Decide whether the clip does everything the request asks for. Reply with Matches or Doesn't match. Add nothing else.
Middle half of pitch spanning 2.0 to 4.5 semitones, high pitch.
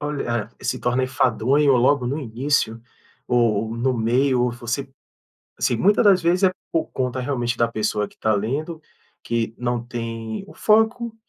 Doesn't match